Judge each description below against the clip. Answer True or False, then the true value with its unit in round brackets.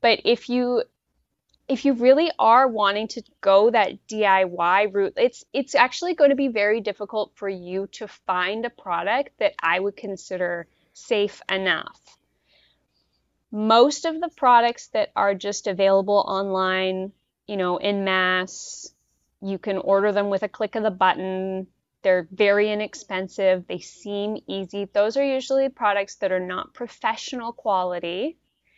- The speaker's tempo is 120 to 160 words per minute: True (150 wpm)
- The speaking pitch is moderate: False (205 Hz)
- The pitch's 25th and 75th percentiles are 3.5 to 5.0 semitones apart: True (4.1 semitones)